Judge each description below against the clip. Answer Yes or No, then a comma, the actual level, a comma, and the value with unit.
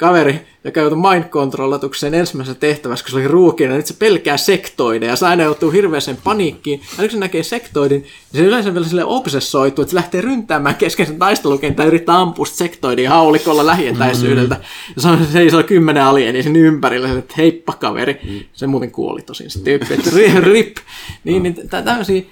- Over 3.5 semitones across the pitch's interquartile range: Yes, average, 4.4 semitones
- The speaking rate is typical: No, fast, 190 wpm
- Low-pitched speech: No, medium, 155 Hz